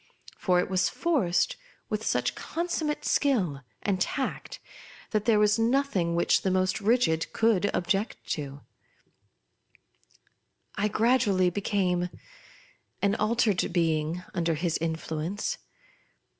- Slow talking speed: Yes, slow, 110 wpm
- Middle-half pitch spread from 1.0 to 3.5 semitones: No, average, 4.8 semitones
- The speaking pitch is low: No, high, 195 Hz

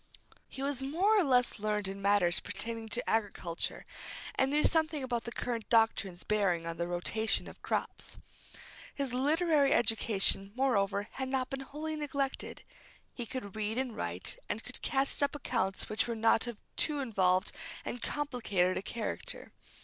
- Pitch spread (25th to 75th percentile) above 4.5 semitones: Yes, average, 5.0 semitones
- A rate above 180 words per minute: No, average, 160 wpm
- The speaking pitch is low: No, high, 235 Hz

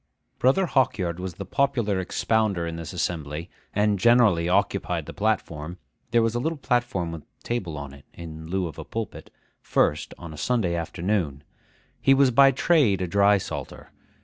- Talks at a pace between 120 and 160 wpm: No, average, 170 wpm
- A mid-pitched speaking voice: No, very low, 95 Hz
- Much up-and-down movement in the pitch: Yes, wide, 6.2 semitones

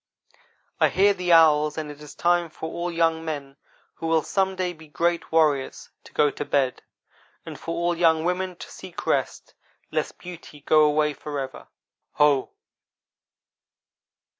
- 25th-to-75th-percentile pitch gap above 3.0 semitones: No, average, 2.7 semitones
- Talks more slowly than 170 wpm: Yes, average, 155 wpm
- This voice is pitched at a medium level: Yes, medium, 160 Hz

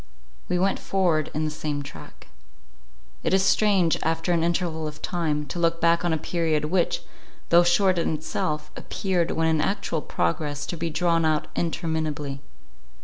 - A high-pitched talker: No, medium, 165 Hz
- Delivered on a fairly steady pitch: Yes, narrow, 2.2 semitones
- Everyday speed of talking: Yes, average, 165 wpm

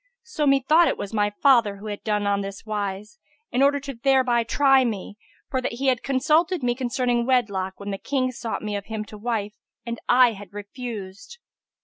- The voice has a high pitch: Yes, high, 235 Hz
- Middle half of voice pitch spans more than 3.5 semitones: Yes, average, 4.4 semitones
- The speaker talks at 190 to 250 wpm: Yes, average, 200 wpm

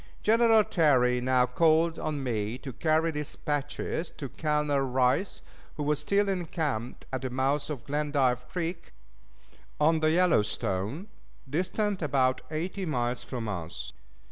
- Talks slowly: Yes, slow, 130 wpm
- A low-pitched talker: No, medium, 150 Hz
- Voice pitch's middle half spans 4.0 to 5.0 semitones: Yes, average, 4.5 semitones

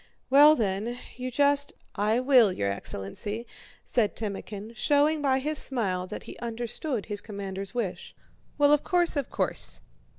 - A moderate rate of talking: Yes, average, 145 wpm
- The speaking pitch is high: Yes, high, 235 Hz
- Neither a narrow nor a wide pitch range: No, wide, 5.9 semitones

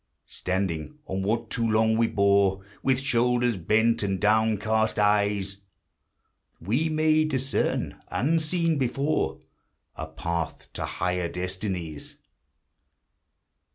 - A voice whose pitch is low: Yes, low, 110 Hz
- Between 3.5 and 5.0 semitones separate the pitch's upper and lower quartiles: Yes, average, 4.6 semitones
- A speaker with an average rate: No, slow, 110 wpm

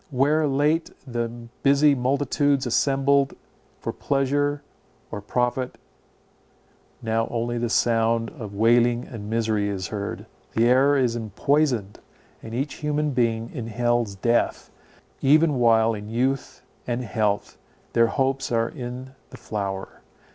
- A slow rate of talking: Yes, slow, 125 wpm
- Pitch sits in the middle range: No, low, 120 Hz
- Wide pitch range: No, average, 3.4 semitones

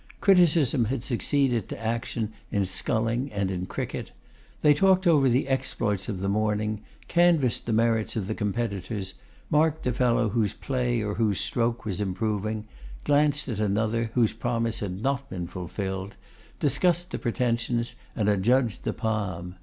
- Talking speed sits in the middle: Yes, average, 155 wpm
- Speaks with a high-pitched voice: No, low, 115 Hz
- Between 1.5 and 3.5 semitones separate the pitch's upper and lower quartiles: No, average, 4.1 semitones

